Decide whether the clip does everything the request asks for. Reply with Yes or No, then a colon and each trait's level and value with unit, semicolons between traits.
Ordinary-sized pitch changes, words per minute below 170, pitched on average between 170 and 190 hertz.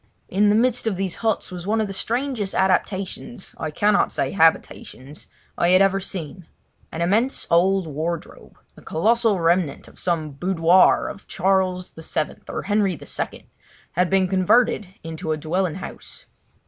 Yes: average, 3.3 semitones; average, 145 wpm; medium, 185 Hz